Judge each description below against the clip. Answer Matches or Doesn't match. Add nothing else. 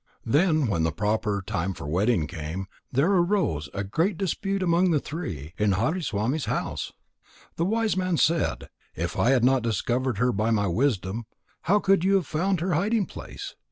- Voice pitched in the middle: Doesn't match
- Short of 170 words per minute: Doesn't match